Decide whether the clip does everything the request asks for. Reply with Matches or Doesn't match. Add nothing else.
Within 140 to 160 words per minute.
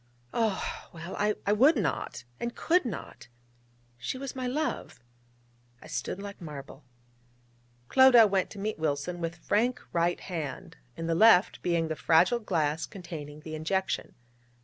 Matches